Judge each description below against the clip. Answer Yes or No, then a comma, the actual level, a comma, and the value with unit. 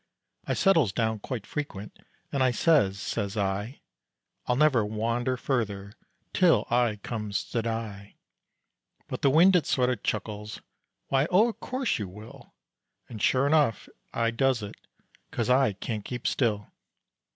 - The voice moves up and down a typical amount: Yes, average, 4.3 semitones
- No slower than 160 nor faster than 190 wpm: No, average, 140 wpm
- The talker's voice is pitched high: No, low, 115 Hz